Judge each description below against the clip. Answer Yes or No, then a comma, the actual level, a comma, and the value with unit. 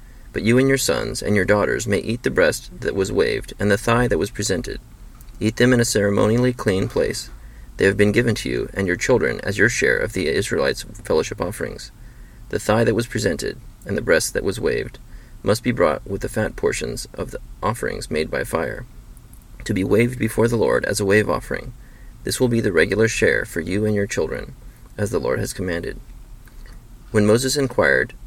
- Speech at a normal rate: No, fast, 210 wpm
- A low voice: Yes, low, 110 Hz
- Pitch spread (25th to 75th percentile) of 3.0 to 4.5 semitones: No, narrow, 2.5 semitones